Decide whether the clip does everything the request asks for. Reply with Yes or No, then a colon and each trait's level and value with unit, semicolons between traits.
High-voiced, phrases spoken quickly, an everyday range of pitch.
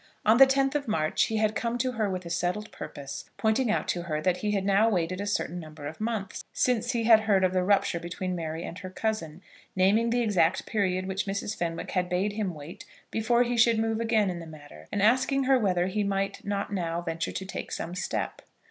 Yes: high, 195 Hz; fast, 230 wpm; average, 4.0 semitones